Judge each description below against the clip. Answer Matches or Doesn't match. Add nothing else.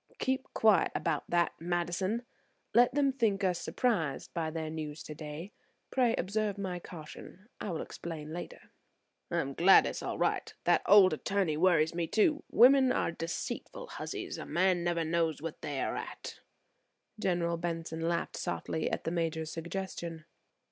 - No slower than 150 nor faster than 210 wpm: Matches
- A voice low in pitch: Doesn't match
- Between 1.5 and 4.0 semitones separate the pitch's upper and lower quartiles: Matches